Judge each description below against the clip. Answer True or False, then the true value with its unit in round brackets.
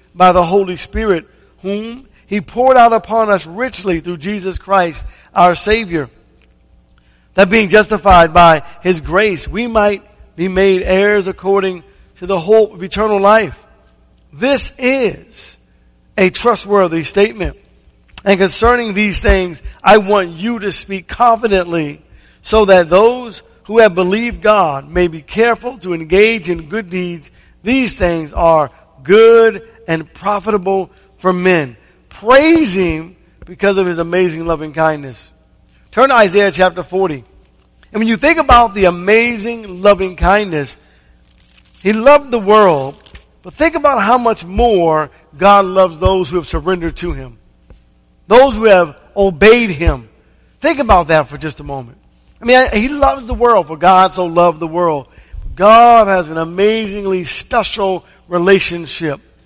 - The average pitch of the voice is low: False (190 Hz)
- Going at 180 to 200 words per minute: False (145 wpm)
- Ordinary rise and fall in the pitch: True (4.4 semitones)